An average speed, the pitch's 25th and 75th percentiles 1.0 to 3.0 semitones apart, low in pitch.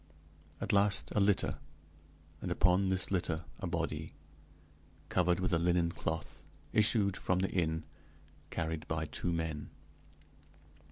No: slow, 125 wpm; narrow, 2.6 semitones; very low, 85 Hz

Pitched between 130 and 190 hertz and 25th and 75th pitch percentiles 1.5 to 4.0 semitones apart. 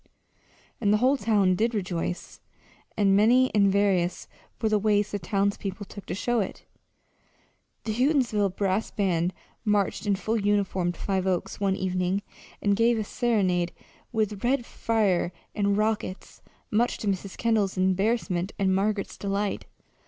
No: high, 200 Hz; narrow, 2.4 semitones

